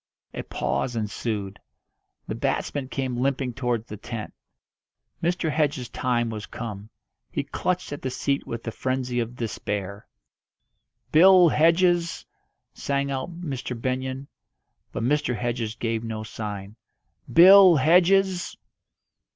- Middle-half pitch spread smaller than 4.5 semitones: No, wide, 5.4 semitones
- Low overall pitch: Yes, low, 130 Hz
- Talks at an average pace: No, slow, 120 wpm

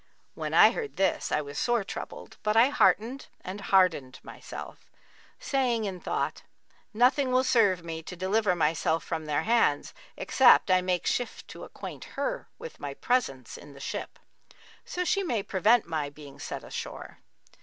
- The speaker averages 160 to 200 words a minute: Yes, average, 165 wpm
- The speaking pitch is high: Yes, high, 195 Hz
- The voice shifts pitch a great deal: Yes, wide, 7.2 semitones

